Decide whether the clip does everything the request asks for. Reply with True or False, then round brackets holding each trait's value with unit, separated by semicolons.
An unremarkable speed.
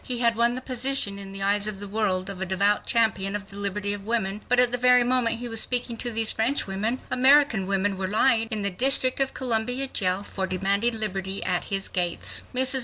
False (230 wpm)